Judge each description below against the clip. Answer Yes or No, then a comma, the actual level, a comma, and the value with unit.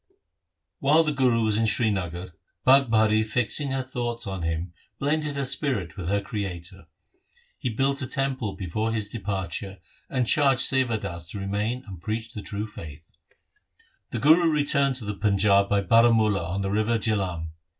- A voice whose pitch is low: Yes, low, 110 Hz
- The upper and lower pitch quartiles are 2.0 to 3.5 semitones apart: No, average, 4.9 semitones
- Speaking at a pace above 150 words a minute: Yes, average, 165 wpm